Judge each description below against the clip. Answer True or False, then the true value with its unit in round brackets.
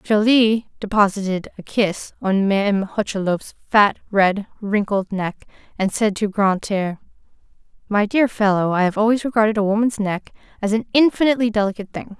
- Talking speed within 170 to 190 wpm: False (150 wpm)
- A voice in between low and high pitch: False (205 Hz)